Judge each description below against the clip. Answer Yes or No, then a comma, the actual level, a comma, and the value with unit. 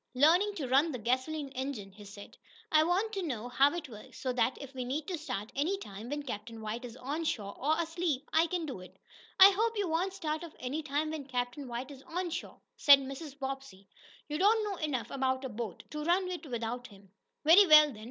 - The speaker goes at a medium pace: No, fast, 225 wpm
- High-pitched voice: Yes, very high, 280 Hz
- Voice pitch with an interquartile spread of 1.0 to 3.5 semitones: No, average, 4.8 semitones